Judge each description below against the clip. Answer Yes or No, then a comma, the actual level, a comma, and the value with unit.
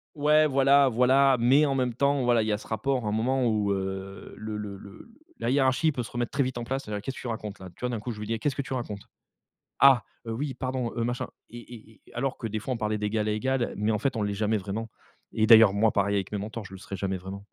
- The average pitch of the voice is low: Yes, low, 115 Hz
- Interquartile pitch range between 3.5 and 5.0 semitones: Yes, average, 3.8 semitones